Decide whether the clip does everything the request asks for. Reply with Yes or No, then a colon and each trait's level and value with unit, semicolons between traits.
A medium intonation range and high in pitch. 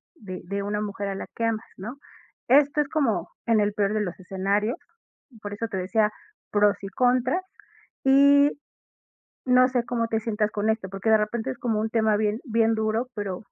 Yes: average, 3.0 semitones; high, 220 Hz